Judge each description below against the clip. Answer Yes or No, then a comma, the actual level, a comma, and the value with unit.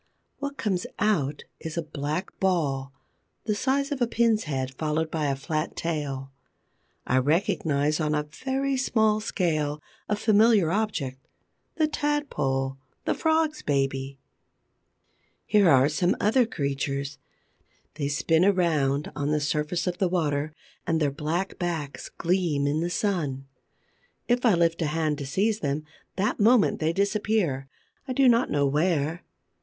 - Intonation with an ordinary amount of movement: No, wide, 6.4 semitones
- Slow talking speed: No, average, 145 wpm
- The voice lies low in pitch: No, medium, 160 Hz